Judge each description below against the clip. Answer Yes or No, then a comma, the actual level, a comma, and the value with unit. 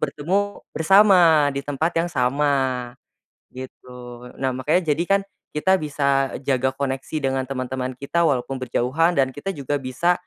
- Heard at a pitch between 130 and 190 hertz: Yes, medium, 140 Hz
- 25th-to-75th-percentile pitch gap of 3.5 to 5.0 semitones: Yes, average, 3.9 semitones